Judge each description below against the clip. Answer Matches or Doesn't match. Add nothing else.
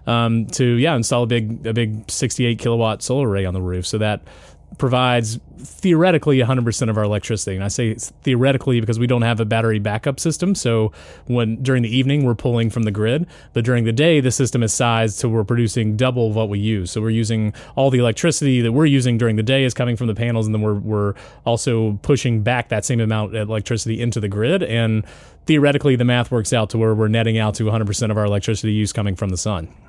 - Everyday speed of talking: Doesn't match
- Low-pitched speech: Matches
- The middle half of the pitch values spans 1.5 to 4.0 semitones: Matches